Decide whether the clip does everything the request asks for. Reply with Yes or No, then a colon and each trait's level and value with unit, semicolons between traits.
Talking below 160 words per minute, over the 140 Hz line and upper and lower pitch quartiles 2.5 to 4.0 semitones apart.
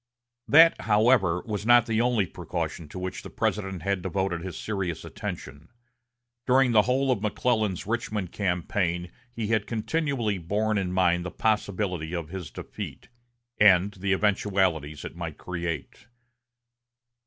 No: average, 140 wpm; low, 100 Hz; average, 3.7 semitones